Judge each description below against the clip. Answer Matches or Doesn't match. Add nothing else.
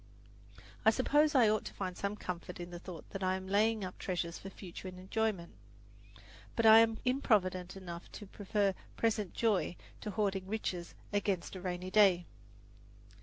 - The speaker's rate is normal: Matches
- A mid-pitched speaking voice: Doesn't match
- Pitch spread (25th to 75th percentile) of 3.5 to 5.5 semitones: Doesn't match